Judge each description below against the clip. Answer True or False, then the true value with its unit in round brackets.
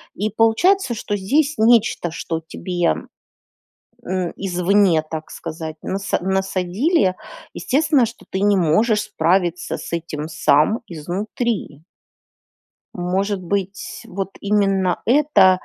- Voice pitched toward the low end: False (190 Hz)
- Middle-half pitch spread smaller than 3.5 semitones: False (3.8 semitones)